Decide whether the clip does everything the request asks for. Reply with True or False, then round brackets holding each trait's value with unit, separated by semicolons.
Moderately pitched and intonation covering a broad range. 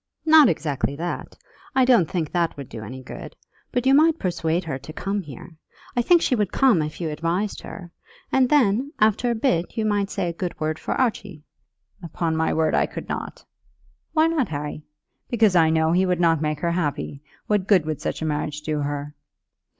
True (170 Hz; 5.9 semitones)